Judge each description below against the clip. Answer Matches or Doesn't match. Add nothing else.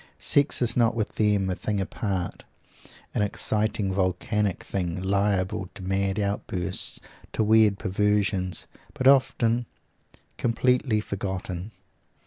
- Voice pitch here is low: Matches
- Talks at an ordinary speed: Doesn't match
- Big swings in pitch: Doesn't match